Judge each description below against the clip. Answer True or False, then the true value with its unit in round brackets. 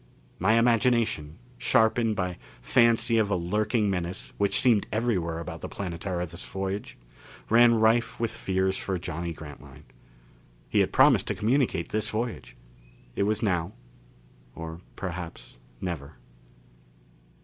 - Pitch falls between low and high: False (95 Hz)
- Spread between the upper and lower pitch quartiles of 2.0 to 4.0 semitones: False (4.7 semitones)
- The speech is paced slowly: True (125 wpm)